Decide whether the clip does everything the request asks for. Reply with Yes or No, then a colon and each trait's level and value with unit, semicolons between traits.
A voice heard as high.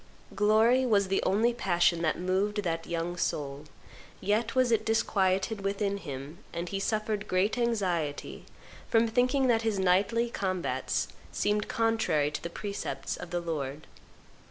Yes: high, 195 Hz